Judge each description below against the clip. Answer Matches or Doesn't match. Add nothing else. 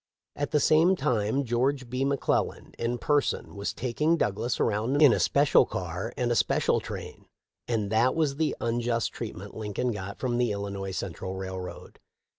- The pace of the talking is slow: Doesn't match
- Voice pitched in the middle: Doesn't match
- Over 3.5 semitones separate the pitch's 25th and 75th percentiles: Matches